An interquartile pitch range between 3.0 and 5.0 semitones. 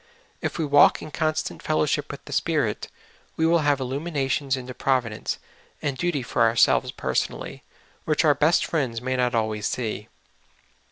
Yes: average, 3.8 semitones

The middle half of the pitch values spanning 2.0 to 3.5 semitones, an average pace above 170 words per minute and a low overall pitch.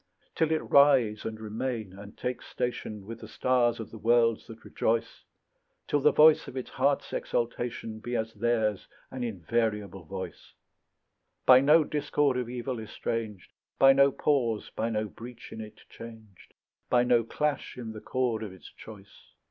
No: average, 2.9 semitones; average, 165 wpm; low, 115 Hz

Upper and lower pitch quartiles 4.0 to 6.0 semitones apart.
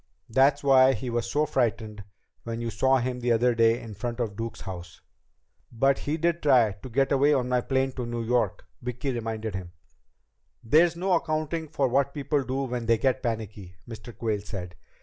No: average, 3.2 semitones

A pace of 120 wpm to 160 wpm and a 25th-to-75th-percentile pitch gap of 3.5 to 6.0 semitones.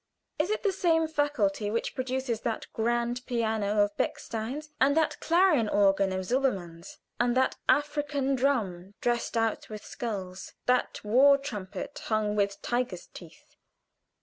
Yes: average, 140 wpm; average, 5.2 semitones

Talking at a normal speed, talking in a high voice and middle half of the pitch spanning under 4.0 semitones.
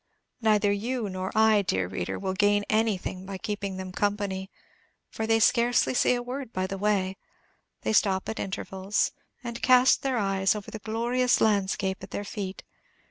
Yes: average, 170 wpm; high, 205 Hz; average, 2.8 semitones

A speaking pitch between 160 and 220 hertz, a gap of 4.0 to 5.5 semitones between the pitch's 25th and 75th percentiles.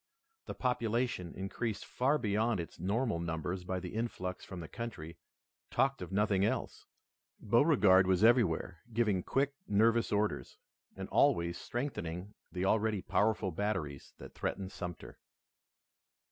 No: low, 100 Hz; average, 4.3 semitones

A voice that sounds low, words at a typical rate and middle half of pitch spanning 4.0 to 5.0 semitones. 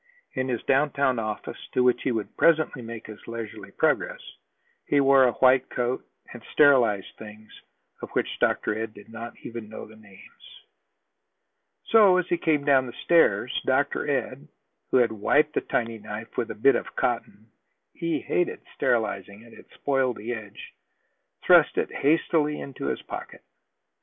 Yes: low, 120 Hz; average, 160 wpm; average, 4.3 semitones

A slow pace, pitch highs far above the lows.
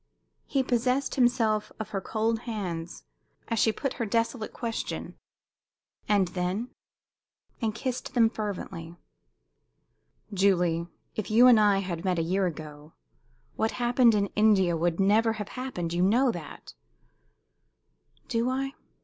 No: slow, 130 wpm; average, 4.7 semitones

